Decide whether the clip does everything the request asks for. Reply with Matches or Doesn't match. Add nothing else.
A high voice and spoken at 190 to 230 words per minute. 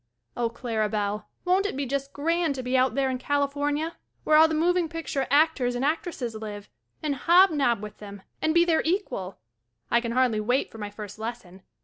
Matches